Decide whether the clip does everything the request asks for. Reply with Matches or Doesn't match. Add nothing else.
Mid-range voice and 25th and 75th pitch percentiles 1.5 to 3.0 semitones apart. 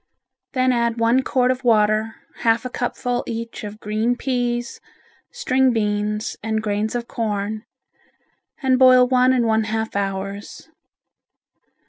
Doesn't match